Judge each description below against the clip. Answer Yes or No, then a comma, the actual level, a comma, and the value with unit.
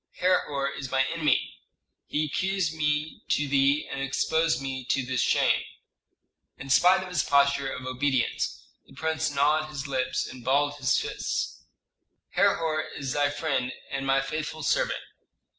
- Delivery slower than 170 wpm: Yes, average, 150 wpm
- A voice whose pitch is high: No, medium, 145 Hz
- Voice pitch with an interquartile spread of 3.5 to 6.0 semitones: No, narrow, 2.5 semitones